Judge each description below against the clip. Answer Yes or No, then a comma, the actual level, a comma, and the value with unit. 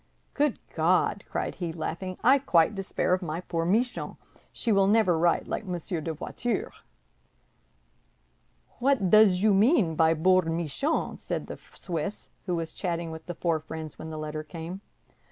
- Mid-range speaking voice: Yes, medium, 175 Hz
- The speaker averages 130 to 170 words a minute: Yes, average, 160 wpm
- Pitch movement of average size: Yes, average, 3.8 semitones